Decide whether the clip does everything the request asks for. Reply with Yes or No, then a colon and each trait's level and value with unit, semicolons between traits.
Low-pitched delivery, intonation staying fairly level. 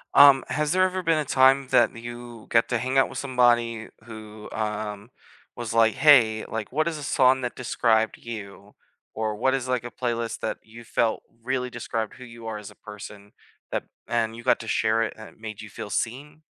No: low, 115 Hz; average, 3.0 semitones